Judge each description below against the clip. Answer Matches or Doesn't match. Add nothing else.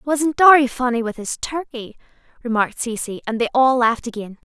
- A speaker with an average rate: Matches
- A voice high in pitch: Matches